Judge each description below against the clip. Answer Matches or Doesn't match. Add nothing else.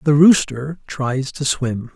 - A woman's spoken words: Doesn't match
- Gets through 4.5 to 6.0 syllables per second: Doesn't match